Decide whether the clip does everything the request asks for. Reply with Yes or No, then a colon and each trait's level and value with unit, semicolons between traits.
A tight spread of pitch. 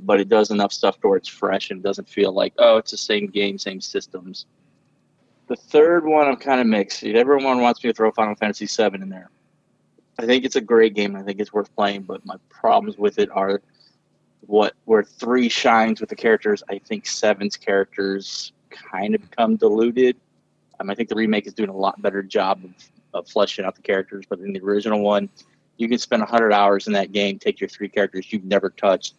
No: average, 3.5 semitones